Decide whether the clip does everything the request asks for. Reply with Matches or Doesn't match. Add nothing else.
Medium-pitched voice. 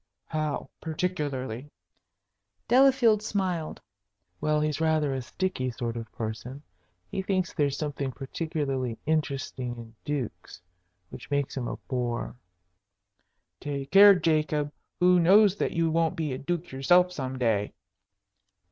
Matches